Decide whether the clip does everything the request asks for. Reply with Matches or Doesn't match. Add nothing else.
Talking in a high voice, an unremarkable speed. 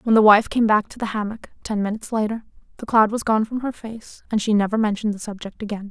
Doesn't match